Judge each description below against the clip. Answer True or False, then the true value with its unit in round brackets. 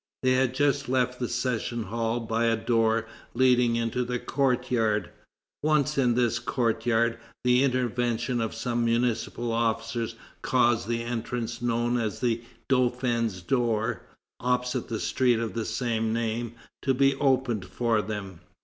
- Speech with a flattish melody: True (1.6 semitones)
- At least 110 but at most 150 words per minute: True (140 wpm)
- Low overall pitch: True (120 Hz)